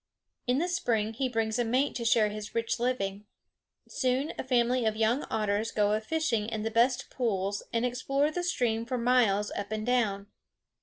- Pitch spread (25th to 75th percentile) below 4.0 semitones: Yes, average, 2.9 semitones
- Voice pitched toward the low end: No, high, 230 Hz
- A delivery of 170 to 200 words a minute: Yes, average, 190 wpm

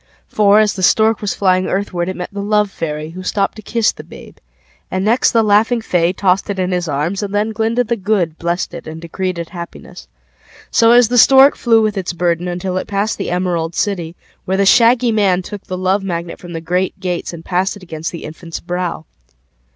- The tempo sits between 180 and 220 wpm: Yes, average, 185 wpm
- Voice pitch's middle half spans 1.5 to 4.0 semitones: Yes, average, 3.3 semitones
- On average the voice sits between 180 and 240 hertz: Yes, medium, 185 Hz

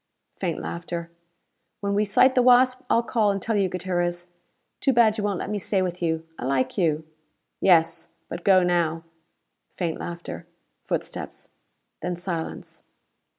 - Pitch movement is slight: No, average, 3.5 semitones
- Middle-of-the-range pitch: Yes, medium, 180 Hz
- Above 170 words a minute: No, average, 150 wpm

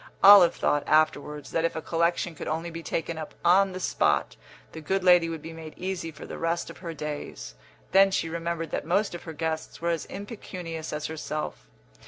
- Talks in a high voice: No, medium, 165 Hz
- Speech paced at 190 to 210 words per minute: Yes, fast, 205 wpm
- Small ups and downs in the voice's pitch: Yes, narrow, 1.9 semitones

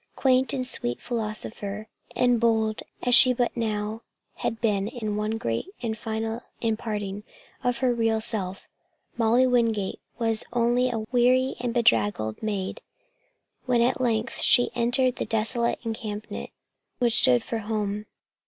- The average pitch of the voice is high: Yes, high, 225 Hz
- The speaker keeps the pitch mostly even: Yes, narrow, 2.3 semitones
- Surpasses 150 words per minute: No, average, 145 wpm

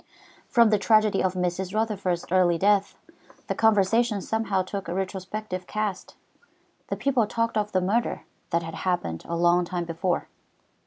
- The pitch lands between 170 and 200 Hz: Yes, high, 190 Hz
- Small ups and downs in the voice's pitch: No, average, 3.2 semitones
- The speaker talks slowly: No, average, 155 wpm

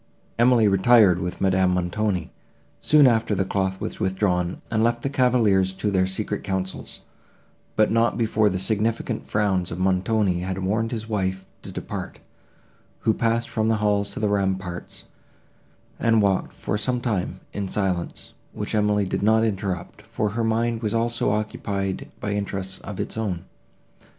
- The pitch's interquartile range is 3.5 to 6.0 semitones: No, average, 2.8 semitones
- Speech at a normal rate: Yes, average, 160 wpm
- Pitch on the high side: No, low, 105 Hz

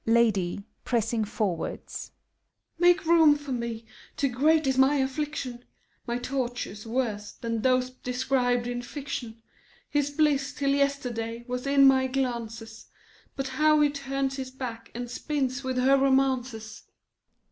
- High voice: Yes, very high, 255 Hz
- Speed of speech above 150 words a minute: No, average, 140 wpm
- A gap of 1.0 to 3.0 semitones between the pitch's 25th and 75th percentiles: Yes, average, 2.7 semitones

